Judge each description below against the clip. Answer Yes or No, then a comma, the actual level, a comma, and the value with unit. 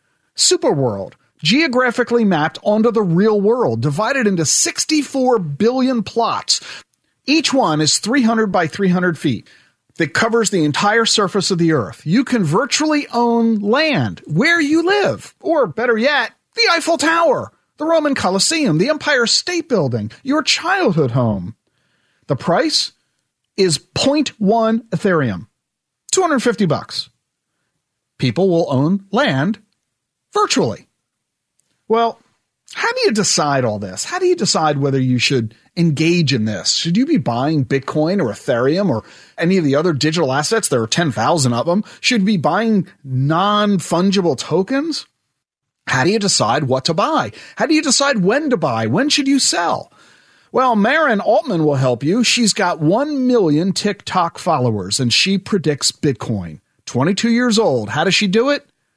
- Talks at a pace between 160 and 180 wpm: No, average, 150 wpm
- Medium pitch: No, high, 195 Hz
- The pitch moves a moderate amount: No, wide, 8.6 semitones